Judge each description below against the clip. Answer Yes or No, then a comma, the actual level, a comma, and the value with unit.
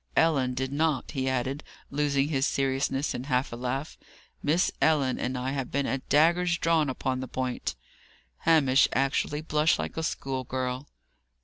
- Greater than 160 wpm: No, average, 155 wpm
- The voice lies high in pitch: No, low, 135 Hz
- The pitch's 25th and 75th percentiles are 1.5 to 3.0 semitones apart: Yes, narrow, 2.5 semitones